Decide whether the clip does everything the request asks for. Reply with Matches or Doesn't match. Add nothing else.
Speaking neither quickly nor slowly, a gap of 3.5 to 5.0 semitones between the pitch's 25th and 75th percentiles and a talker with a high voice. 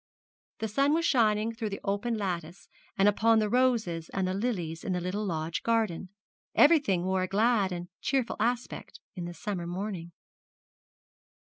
Matches